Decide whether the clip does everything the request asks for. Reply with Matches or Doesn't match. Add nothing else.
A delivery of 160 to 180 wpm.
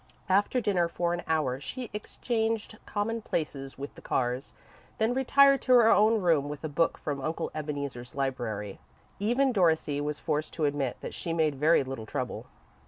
Matches